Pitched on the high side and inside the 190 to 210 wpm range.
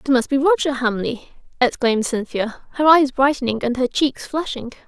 No: very high, 270 Hz; average, 170 wpm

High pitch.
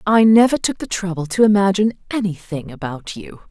Yes: high, 195 Hz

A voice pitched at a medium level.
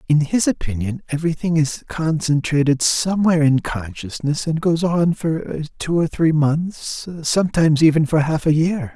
Yes: medium, 155 Hz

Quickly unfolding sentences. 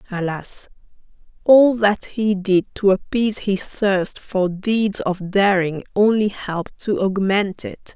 No: slow, 135 wpm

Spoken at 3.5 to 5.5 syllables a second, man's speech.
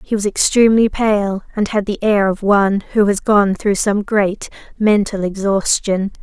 No: 4.6 syllables/s; female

